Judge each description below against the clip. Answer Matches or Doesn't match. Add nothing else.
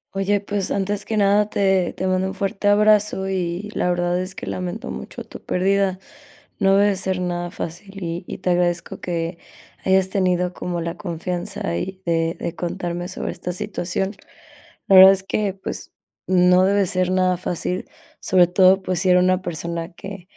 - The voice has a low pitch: Doesn't match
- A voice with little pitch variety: Matches